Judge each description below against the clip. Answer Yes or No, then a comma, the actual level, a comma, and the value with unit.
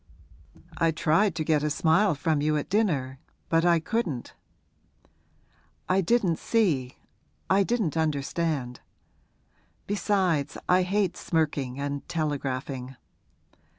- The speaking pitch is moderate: Yes, medium, 160 Hz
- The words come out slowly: Yes, slow, 110 wpm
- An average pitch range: Yes, average, 4.7 semitones